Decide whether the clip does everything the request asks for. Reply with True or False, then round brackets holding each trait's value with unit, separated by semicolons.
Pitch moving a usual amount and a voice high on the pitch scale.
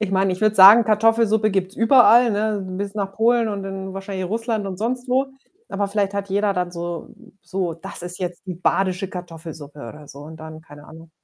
True (3.4 semitones; 195 Hz)